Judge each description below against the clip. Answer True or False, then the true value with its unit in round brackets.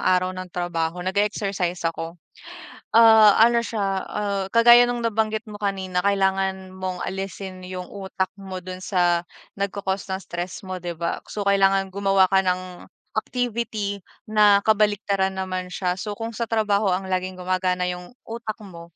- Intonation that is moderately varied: False (2.1 semitones)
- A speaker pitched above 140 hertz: True (190 Hz)